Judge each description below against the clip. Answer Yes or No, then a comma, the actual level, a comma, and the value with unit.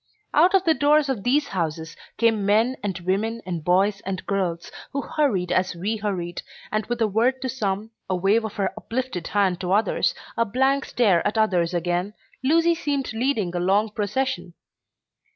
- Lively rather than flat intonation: Yes, wide, 5.7 semitones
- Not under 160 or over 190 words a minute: Yes, average, 180 wpm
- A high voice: Yes, high, 210 Hz